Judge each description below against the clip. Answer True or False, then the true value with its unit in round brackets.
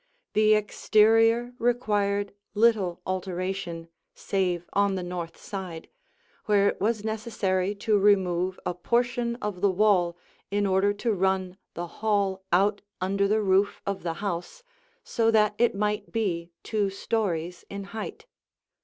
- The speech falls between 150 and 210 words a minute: False (135 wpm)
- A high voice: True (200 Hz)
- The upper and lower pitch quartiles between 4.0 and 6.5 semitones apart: False (2.6 semitones)